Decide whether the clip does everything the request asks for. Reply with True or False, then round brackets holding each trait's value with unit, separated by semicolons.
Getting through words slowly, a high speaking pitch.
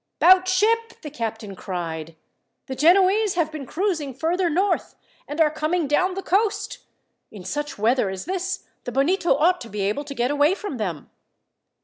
False (170 wpm; 300 Hz)